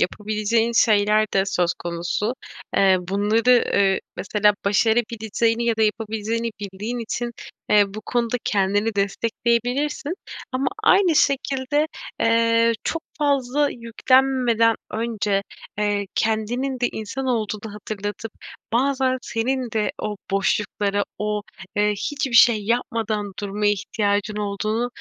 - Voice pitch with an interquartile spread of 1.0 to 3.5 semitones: Yes, average, 2.8 semitones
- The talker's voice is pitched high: Yes, high, 220 Hz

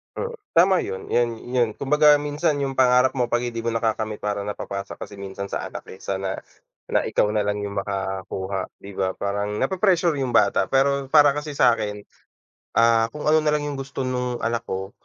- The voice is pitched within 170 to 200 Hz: No, low, 120 Hz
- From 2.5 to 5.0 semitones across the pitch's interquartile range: No, wide, 5.6 semitones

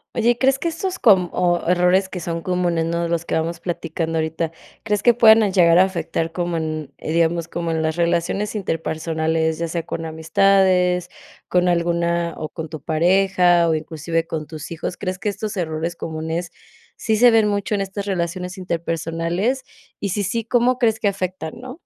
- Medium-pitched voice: Yes, medium, 175 Hz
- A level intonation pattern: No, average, 3.1 semitones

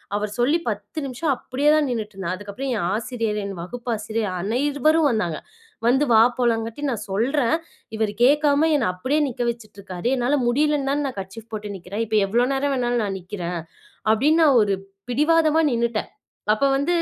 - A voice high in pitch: Yes, high, 235 Hz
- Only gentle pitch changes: No, average, 5.3 semitones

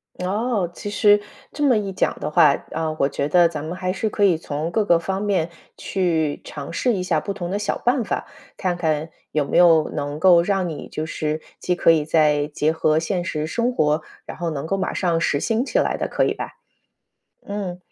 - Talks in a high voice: No, medium, 175 Hz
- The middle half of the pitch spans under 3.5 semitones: No, average, 4.1 semitones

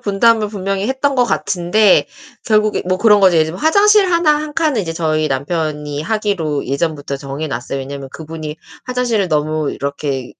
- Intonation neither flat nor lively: No, wide, 6.6 semitones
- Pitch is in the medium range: Yes, medium, 175 Hz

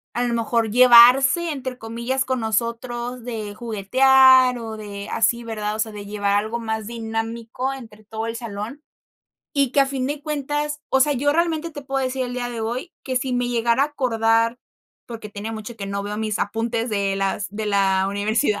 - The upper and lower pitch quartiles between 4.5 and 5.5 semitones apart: No, average, 3.2 semitones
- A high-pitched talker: Yes, high, 235 Hz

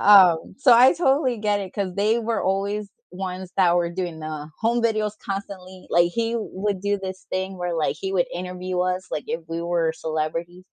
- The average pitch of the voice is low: No, medium, 185 Hz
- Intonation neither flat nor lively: Yes, average, 3.0 semitones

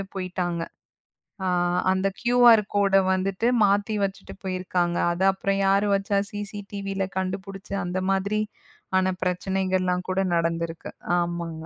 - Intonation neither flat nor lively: No, narrow, 1.6 semitones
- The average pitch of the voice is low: No, high, 190 Hz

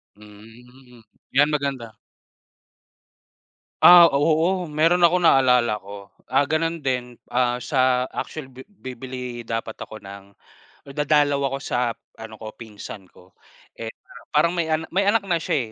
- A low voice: Yes, low, 130 Hz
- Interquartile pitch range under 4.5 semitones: No, average, 5.3 semitones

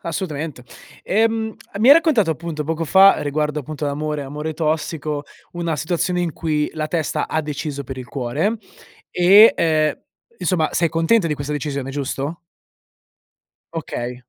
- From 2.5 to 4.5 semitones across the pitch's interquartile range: Yes, average, 2.9 semitones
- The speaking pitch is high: No, medium, 155 Hz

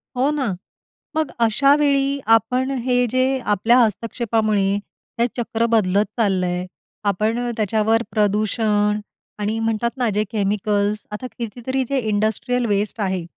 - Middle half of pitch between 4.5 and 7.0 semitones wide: No, average, 3.0 semitones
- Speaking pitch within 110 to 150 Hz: No, high, 220 Hz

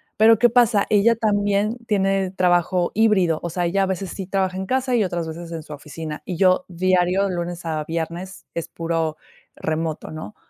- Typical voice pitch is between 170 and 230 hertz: Yes, medium, 185 Hz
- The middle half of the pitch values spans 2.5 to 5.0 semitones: Yes, average, 3.1 semitones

